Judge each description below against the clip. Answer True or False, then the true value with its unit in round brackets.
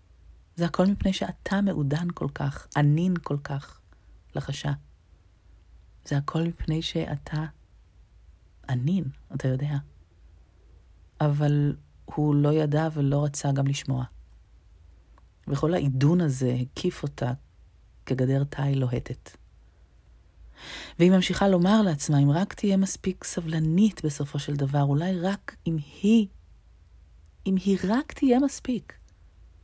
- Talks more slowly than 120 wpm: True (110 wpm)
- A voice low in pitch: False (145 Hz)